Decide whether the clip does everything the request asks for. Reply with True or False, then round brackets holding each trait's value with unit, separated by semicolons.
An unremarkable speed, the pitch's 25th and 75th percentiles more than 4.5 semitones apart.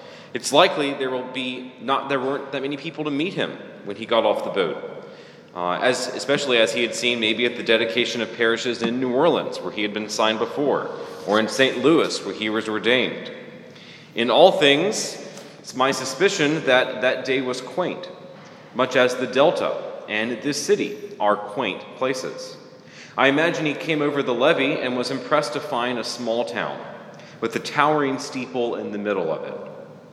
True (190 wpm; 5.5 semitones)